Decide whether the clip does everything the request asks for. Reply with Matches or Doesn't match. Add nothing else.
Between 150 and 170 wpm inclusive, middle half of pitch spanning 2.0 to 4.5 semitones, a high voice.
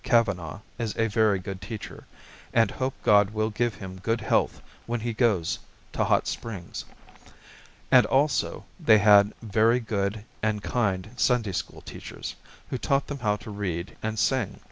Doesn't match